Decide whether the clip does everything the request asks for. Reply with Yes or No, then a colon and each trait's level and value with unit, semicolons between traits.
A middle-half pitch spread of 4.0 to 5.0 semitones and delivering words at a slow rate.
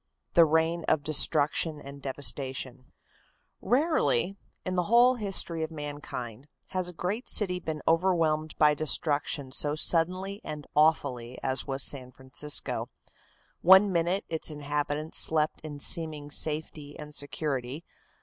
No: average, 3.1 semitones; slow, 130 wpm